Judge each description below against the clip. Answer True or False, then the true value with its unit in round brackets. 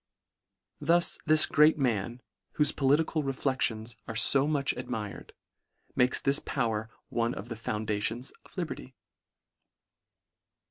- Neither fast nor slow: False (120 wpm)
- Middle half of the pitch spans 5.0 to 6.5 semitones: False (4.6 semitones)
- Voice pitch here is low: True (125 Hz)